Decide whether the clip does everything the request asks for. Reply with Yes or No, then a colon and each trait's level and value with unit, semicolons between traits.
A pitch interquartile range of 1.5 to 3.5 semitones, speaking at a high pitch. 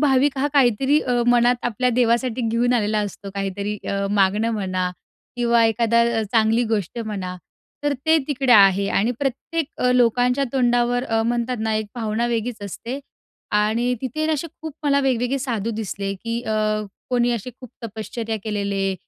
Yes: average, 3.0 semitones; high, 235 Hz